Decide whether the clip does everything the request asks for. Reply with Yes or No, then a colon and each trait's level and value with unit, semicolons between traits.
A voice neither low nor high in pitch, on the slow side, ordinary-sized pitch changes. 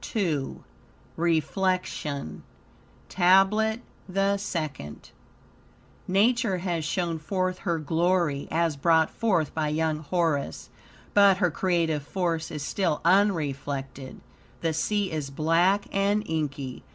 Yes: medium, 170 Hz; slow, 105 wpm; average, 4.0 semitones